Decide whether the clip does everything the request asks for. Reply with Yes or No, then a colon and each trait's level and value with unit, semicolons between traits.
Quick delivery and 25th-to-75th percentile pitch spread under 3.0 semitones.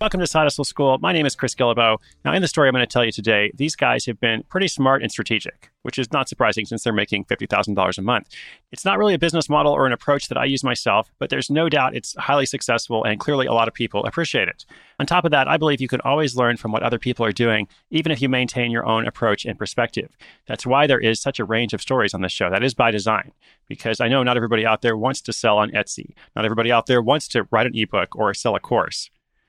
No: fast, 265 wpm; average, 3.7 semitones